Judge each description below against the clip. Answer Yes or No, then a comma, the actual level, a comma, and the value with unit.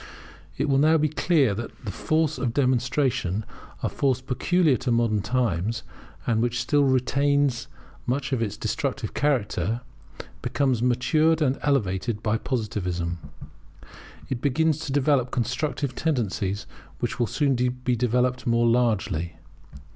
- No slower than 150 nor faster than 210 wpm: No, average, 140 wpm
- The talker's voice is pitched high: No, low, 125 Hz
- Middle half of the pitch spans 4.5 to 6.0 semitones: No, average, 3.9 semitones